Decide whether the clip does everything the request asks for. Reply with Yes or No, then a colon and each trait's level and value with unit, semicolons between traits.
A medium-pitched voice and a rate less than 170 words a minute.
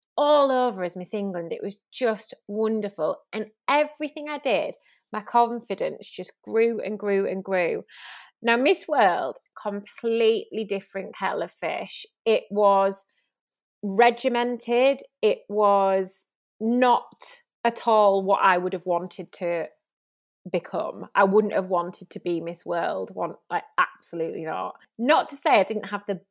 No: high, 215 Hz; average, 145 wpm